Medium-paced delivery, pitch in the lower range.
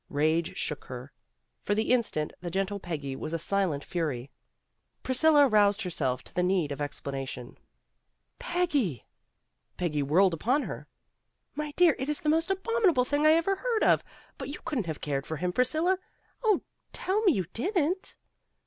No: average, 180 wpm; high, 200 Hz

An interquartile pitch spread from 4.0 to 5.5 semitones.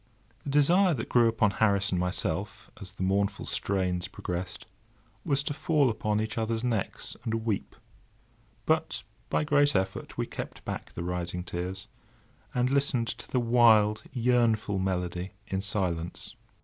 Yes: average, 4.6 semitones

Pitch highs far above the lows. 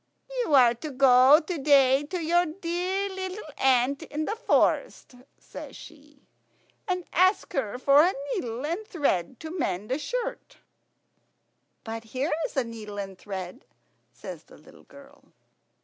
Yes: wide, 5.9 semitones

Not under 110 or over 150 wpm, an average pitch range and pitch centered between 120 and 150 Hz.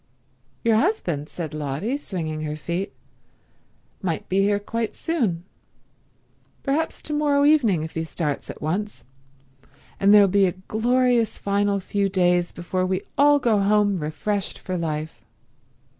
No: average, 140 wpm; average, 4.9 semitones; high, 195 Hz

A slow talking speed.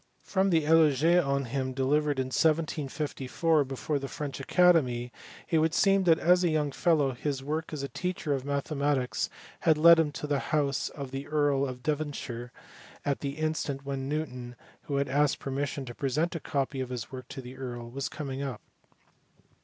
No: average, 190 wpm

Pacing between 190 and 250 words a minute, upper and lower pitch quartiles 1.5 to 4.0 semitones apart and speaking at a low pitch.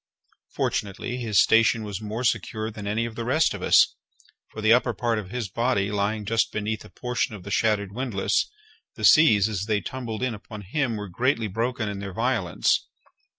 Yes: average, 200 wpm; narrow, 2.5 semitones; low, 110 Hz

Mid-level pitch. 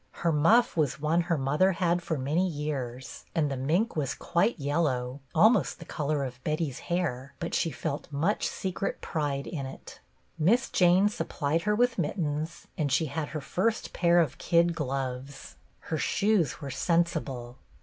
Yes: medium, 155 Hz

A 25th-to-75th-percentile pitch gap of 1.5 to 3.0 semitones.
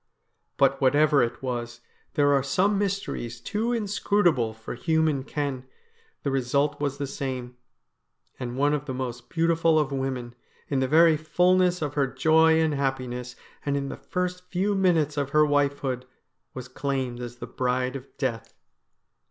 No: average, 3.9 semitones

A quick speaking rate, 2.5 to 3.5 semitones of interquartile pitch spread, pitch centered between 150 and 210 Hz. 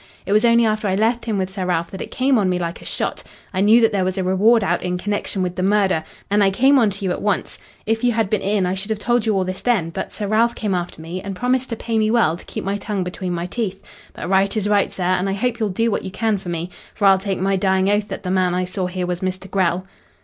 Yes: fast, 300 wpm; average, 2.9 semitones; high, 195 Hz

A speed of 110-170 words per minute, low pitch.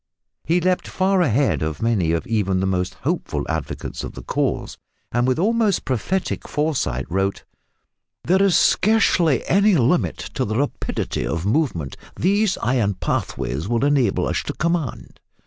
Yes: average, 150 wpm; low, 130 Hz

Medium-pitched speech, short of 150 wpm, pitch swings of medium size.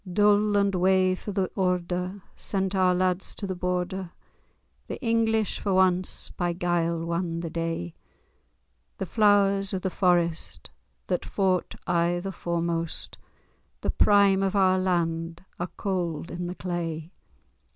No: medium, 180 Hz; average, 140 wpm; narrow, 2.1 semitones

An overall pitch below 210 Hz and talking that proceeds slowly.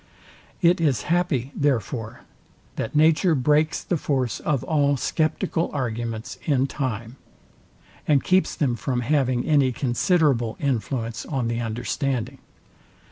Yes: low, 135 Hz; slow, 120 wpm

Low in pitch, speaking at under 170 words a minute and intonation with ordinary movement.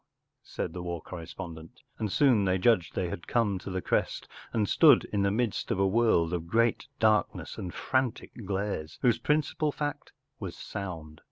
No: low, 100 Hz; average, 185 wpm; average, 4.9 semitones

